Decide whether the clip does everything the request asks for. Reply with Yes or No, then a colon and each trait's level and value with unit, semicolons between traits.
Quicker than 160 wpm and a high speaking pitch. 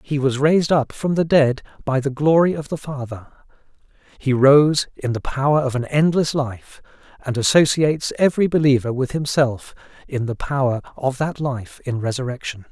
No: average, 170 wpm; medium, 140 Hz